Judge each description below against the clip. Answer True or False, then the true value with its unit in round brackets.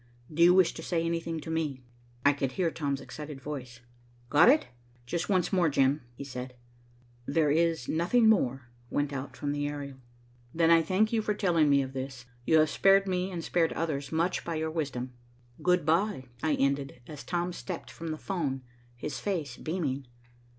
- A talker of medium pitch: True (155 Hz)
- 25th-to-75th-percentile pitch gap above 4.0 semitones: False (3.7 semitones)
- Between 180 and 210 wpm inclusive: True (190 wpm)